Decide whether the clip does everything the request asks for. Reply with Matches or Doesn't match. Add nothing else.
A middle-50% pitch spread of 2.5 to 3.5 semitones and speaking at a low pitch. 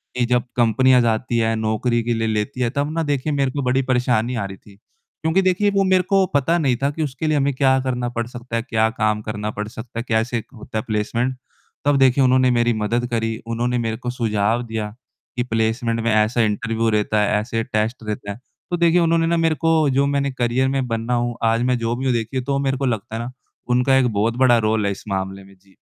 Matches